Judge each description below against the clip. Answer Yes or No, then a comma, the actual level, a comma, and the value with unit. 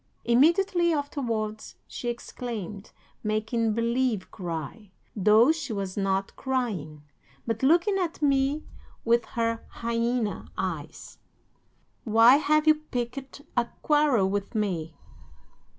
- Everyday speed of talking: No, slow, 105 wpm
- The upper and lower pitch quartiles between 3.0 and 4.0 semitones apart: No, average, 4.8 semitones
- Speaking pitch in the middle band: No, high, 235 Hz